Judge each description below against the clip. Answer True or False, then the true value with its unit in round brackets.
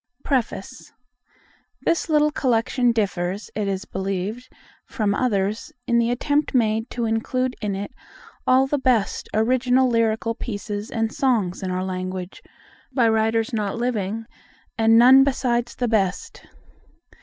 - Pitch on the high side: True (225 Hz)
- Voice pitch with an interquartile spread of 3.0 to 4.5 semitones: True (3.8 semitones)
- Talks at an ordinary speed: False (130 wpm)